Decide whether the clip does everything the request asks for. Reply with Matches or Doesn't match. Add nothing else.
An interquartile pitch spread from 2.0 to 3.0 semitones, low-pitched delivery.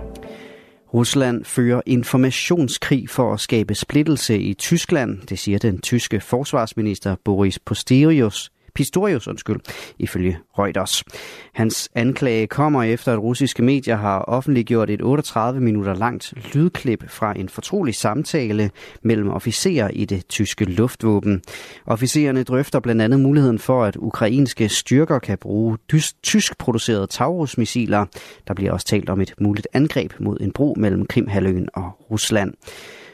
Doesn't match